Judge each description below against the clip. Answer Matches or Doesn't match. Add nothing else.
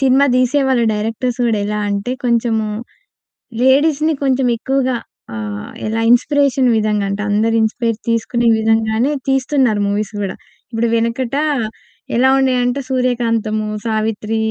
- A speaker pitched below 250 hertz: Matches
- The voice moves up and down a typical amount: Matches